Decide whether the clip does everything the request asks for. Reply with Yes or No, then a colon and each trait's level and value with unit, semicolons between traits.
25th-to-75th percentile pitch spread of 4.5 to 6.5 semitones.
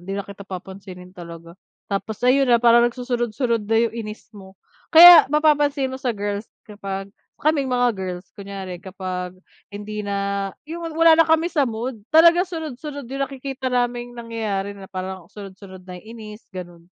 Yes: average, 5.2 semitones